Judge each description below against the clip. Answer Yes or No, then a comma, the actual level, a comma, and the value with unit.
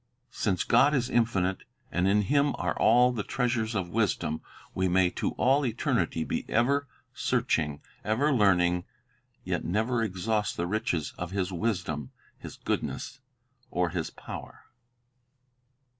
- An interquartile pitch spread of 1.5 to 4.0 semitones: No, average, 5.1 semitones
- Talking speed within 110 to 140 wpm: Yes, slow, 135 wpm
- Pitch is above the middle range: No, low, 105 Hz